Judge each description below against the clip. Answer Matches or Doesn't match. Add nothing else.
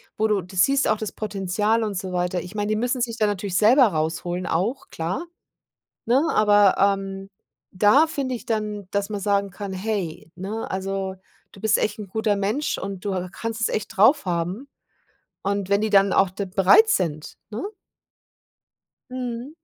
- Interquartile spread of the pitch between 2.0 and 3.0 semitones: Matches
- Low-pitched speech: Doesn't match